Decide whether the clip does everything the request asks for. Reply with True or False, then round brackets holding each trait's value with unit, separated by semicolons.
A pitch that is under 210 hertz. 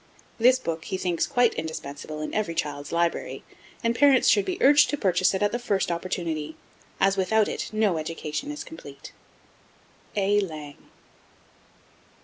True (190 Hz)